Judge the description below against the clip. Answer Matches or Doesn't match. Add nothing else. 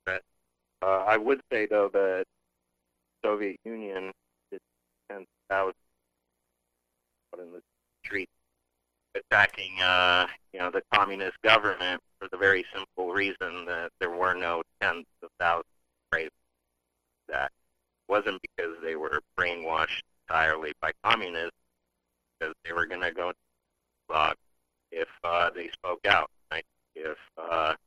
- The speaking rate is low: Matches